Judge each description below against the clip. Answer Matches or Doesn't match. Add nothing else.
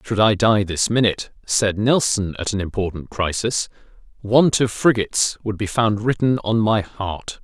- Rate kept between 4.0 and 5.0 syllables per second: Matches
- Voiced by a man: Matches